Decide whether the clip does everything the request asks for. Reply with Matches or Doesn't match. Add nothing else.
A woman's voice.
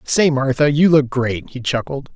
Doesn't match